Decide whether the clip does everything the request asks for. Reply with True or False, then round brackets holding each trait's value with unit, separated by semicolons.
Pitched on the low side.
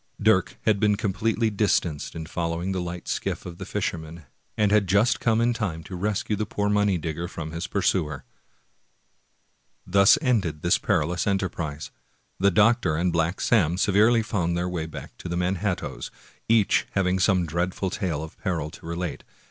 True (90 Hz)